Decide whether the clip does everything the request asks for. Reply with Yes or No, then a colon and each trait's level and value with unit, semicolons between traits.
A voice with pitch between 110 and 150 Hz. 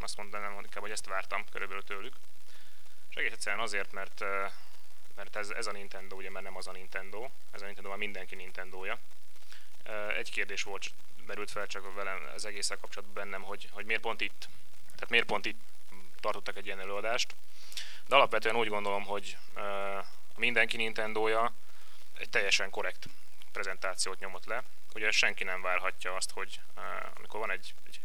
No: low, 100 Hz